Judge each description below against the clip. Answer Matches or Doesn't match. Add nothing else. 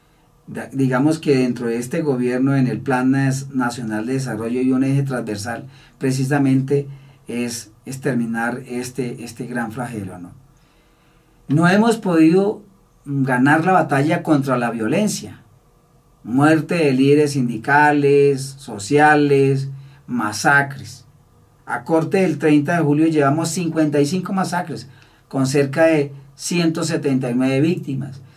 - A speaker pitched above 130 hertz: Matches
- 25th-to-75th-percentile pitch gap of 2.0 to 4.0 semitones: Matches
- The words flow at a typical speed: Doesn't match